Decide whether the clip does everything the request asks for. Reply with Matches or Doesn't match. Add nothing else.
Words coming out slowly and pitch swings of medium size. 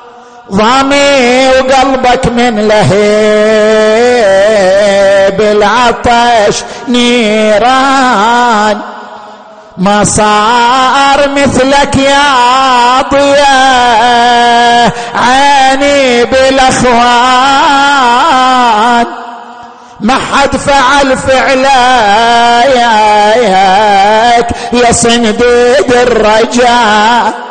Matches